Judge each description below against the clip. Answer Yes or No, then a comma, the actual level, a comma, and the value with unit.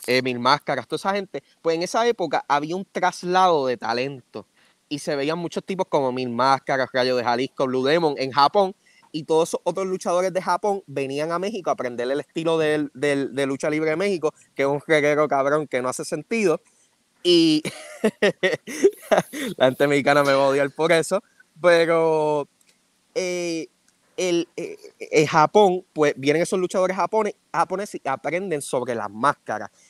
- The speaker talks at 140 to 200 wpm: Yes, average, 175 wpm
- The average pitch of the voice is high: No, medium, 160 Hz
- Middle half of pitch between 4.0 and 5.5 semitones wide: Yes, average, 5.1 semitones